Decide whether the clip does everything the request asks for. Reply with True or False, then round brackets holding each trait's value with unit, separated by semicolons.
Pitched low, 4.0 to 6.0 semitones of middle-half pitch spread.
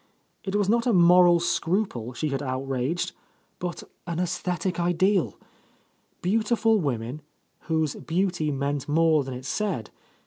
False (170 Hz; 5.0 semitones)